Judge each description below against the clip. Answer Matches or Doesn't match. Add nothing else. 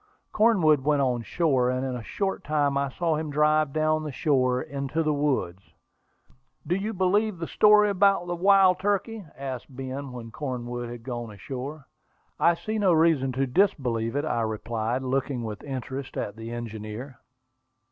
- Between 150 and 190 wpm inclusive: Matches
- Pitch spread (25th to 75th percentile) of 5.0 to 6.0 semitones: Matches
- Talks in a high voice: Doesn't match